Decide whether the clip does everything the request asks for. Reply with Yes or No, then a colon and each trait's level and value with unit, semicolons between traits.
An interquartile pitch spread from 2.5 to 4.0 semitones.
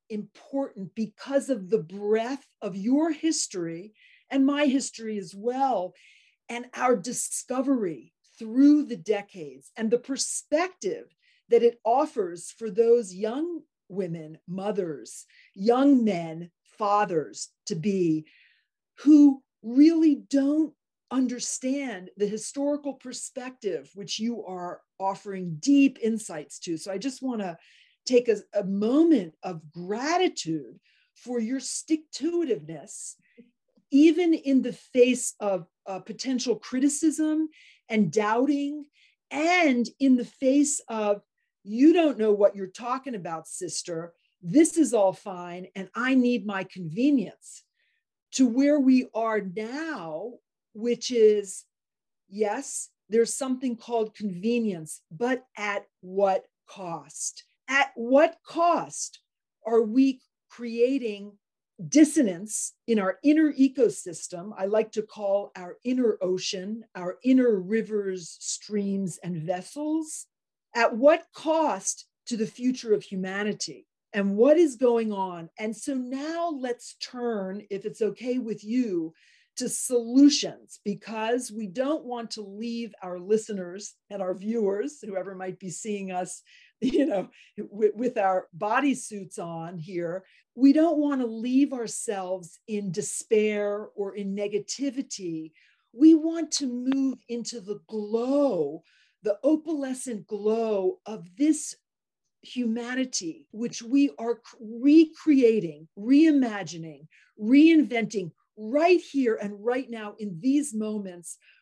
No: wide, 5.5 semitones